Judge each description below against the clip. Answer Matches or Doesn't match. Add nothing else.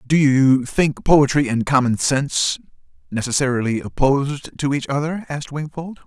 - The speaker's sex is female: Doesn't match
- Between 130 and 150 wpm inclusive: Matches